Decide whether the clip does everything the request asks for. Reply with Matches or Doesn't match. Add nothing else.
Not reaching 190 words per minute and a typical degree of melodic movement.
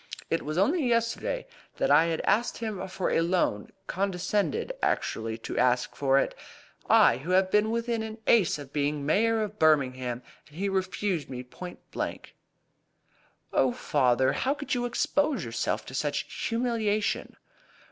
Doesn't match